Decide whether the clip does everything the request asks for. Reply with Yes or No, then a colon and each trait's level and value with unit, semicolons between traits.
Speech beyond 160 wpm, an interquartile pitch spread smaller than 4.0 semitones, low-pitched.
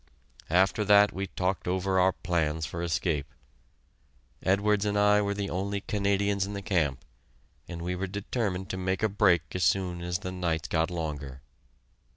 Yes: average, 170 wpm; narrow, 2.6 semitones; very low, 95 Hz